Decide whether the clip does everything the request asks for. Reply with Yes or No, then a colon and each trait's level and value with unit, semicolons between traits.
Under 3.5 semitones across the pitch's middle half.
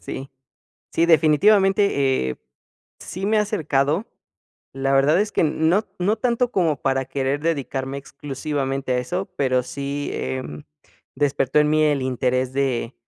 No: average, 4.1 semitones